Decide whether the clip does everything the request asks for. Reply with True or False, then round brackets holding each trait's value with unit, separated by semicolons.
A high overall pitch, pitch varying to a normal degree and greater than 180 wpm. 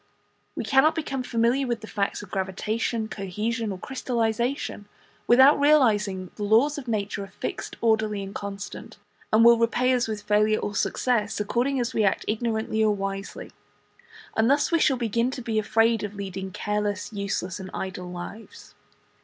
False (220 Hz; 3.0 semitones; 170 wpm)